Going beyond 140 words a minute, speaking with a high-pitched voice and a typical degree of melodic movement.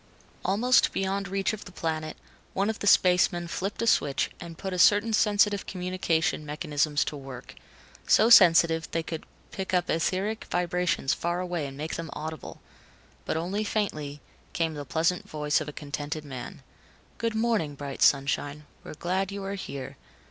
No: average, 165 wpm; medium, 170 Hz; average, 4.4 semitones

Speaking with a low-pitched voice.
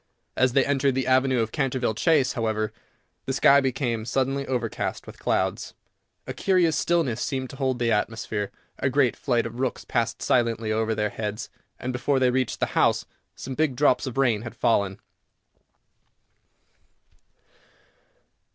Yes: low, 125 Hz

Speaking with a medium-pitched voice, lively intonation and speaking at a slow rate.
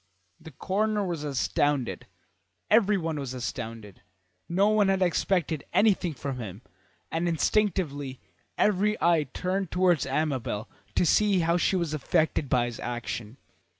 Yes: medium, 160 Hz; wide, 6.3 semitones; slow, 130 wpm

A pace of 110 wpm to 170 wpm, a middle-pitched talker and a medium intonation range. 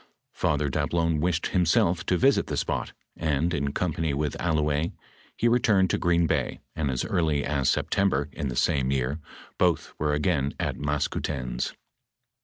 No: average, 160 wpm; very low, 75 Hz; average, 3.4 semitones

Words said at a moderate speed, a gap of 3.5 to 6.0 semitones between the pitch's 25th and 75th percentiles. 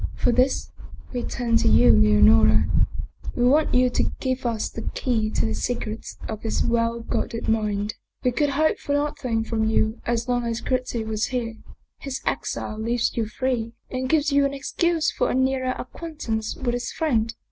No: average, 180 wpm; average, 2.8 semitones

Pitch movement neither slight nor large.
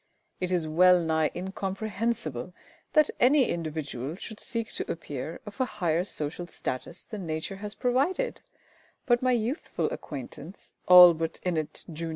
No: wide, 5.8 semitones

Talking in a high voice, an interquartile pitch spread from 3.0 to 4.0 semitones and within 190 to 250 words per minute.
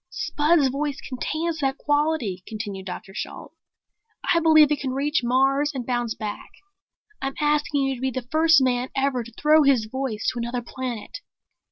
No: very high, 270 Hz; average, 3.6 semitones; average, 170 wpm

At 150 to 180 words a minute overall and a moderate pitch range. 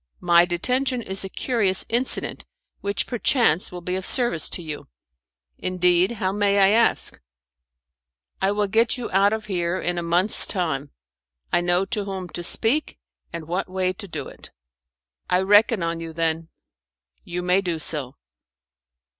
Yes: average, 160 wpm; average, 3.1 semitones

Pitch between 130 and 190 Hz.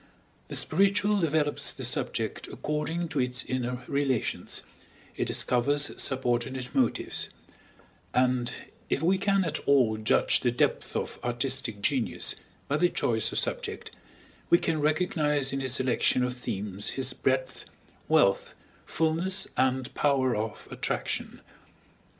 Yes: low, 135 Hz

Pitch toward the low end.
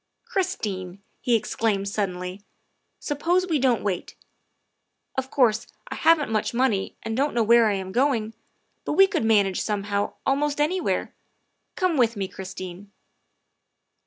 No: high, 225 Hz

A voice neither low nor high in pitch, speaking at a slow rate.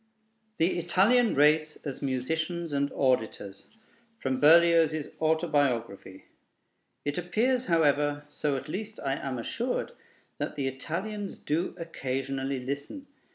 Yes: medium, 150 Hz; slow, 110 wpm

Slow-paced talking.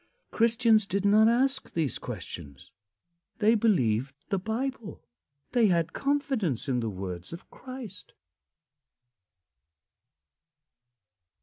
Yes: slow, 95 wpm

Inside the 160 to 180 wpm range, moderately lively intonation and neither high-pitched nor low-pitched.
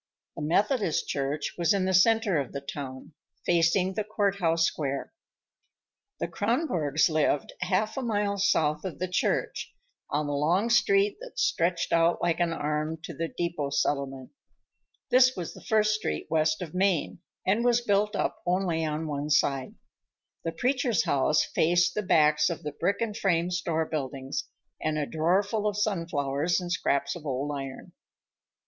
Yes: average, 165 wpm; average, 4.9 semitones; medium, 170 Hz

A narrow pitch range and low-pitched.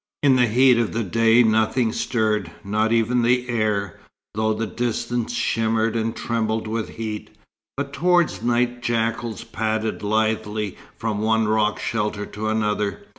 Yes: narrow, 1.5 semitones; low, 110 Hz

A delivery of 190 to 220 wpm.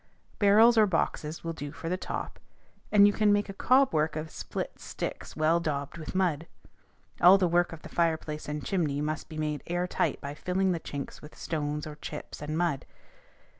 Yes: average, 200 wpm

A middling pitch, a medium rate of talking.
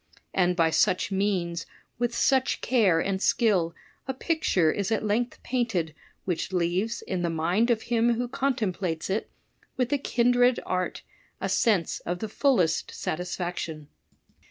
No: high, 195 Hz; average, 155 wpm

